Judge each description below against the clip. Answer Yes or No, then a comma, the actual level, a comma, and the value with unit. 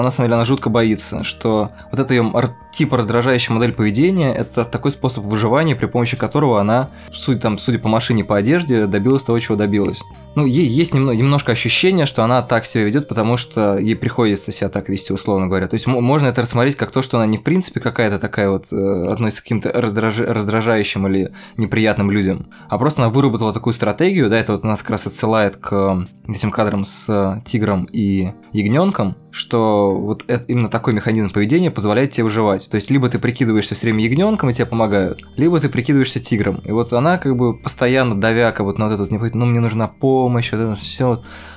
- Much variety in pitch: No, average, 3.2 semitones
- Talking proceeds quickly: Yes, fast, 210 wpm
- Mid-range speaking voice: No, low, 115 Hz